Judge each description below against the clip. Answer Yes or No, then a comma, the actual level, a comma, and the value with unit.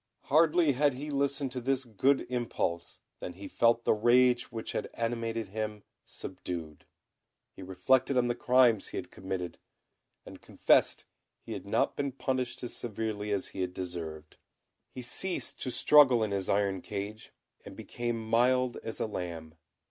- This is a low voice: Yes, low, 115 Hz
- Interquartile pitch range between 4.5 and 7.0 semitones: Yes, average, 4.8 semitones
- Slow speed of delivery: No, average, 160 wpm